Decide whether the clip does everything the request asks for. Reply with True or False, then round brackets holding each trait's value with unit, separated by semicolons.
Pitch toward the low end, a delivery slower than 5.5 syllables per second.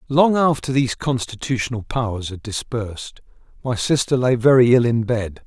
True (120 Hz; 5.2 syllables/s)